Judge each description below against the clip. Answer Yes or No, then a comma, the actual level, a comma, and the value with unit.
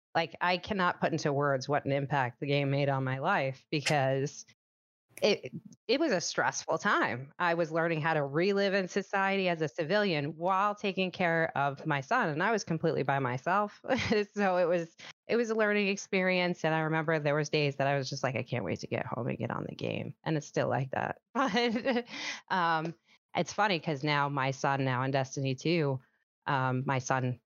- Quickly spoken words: Yes, fast, 210 wpm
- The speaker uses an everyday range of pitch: Yes, average, 4.9 semitones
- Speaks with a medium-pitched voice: Yes, medium, 160 Hz